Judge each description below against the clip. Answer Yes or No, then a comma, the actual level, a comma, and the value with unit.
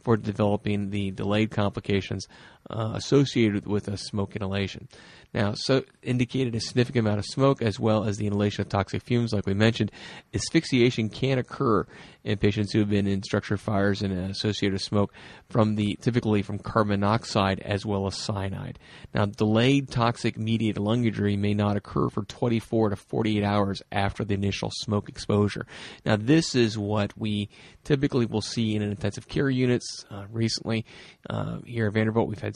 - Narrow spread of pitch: Yes, narrow, 2.2 semitones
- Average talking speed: Yes, average, 175 wpm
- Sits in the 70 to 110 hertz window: Yes, low, 105 Hz